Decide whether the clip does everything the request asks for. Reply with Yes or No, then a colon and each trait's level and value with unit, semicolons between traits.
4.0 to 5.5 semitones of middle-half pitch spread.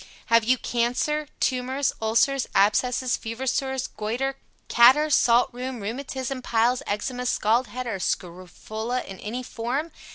No: average, 2.7 semitones